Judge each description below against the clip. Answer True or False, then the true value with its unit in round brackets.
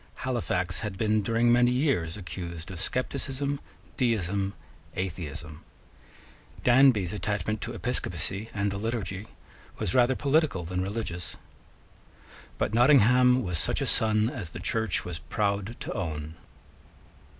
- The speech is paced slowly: True (125 wpm)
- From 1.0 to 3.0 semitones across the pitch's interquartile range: False (5.1 semitones)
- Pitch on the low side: True (105 Hz)